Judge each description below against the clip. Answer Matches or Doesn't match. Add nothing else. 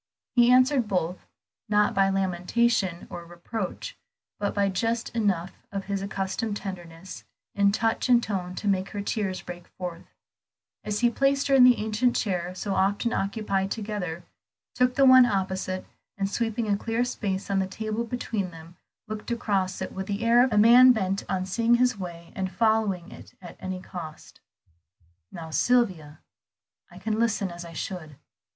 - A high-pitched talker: Matches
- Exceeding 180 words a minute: Doesn't match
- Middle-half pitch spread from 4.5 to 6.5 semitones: Doesn't match